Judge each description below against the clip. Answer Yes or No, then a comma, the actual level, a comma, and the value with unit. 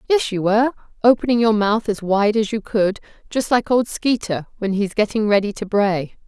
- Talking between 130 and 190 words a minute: No, average, 200 wpm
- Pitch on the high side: Yes, high, 215 Hz